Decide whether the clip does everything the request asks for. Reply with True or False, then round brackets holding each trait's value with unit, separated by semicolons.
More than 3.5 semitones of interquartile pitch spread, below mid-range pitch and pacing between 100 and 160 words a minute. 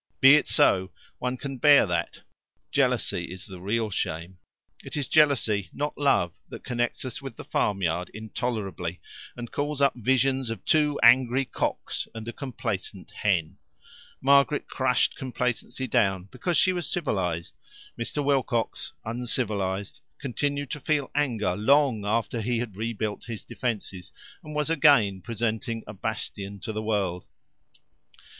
True (5.3 semitones; 115 Hz; 140 wpm)